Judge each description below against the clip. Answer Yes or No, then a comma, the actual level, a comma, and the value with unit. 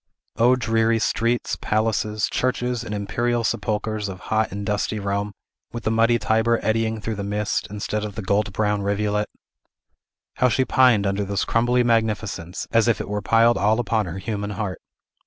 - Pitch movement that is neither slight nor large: No, narrow, 2.0 semitones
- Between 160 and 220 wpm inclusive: Yes, average, 175 wpm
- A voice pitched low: Yes, low, 110 Hz